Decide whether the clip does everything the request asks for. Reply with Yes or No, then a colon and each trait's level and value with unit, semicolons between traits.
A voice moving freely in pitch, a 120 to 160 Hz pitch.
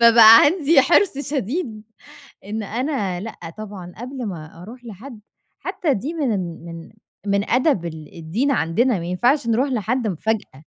No: wide, 6.3 semitones; high, 225 Hz